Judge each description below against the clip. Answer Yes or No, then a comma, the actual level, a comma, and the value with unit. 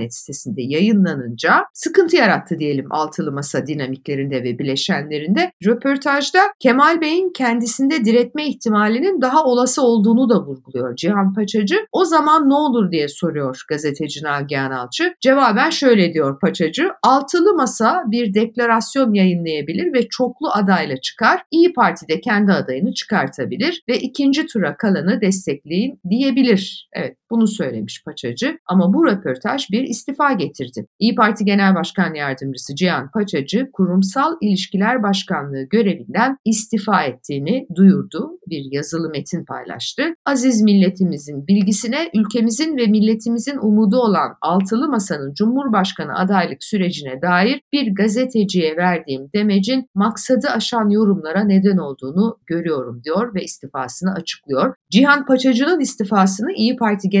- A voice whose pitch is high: Yes, high, 205 Hz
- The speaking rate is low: No, average, 125 wpm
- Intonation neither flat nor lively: No, wide, 7.2 semitones